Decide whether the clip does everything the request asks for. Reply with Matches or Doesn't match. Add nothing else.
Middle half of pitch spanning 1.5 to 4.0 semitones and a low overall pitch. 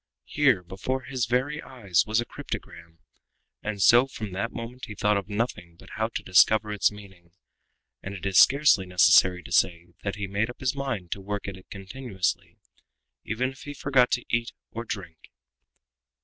Doesn't match